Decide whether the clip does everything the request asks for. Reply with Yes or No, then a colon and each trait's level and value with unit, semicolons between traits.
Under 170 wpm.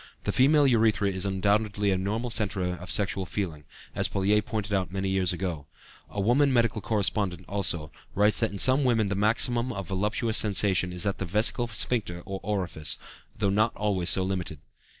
No: average, 180 wpm